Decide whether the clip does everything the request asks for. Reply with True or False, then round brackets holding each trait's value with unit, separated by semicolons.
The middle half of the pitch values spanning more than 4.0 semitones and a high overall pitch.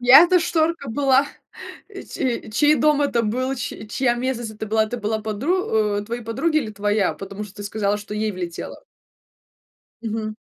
True (4.5 semitones; 230 Hz)